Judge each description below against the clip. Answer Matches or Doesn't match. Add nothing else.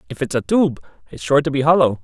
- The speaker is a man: Matches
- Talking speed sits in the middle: Doesn't match